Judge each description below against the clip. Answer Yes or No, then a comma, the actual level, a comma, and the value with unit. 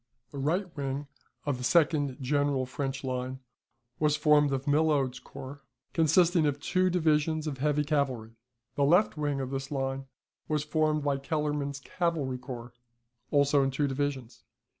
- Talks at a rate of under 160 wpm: Yes, average, 150 wpm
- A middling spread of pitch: No, narrow, 2.1 semitones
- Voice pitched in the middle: Yes, medium, 145 Hz